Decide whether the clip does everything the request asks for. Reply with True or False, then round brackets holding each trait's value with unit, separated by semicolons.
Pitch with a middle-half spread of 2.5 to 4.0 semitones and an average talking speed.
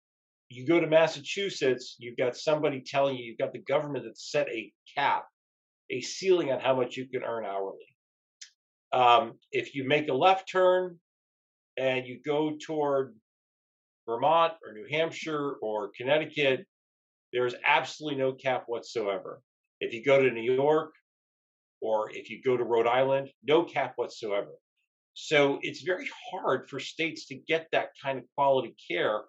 False (4.5 semitones; 160 wpm)